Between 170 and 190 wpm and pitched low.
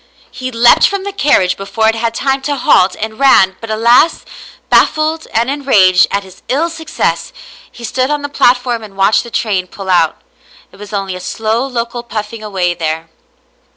No: average, 185 wpm; high, 225 Hz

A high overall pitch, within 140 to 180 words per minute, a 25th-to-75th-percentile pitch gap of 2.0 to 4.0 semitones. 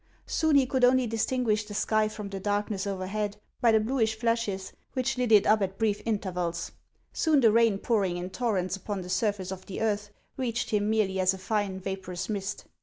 No: high, 210 Hz; average, 200 wpm; average, 2.9 semitones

